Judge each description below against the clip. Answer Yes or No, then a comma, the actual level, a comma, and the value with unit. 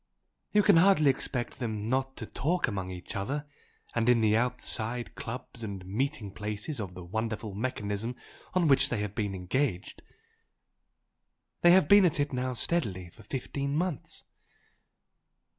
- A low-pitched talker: Yes, low, 120 Hz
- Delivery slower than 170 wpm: Yes, average, 150 wpm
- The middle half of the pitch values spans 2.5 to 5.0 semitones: No, wide, 5.4 semitones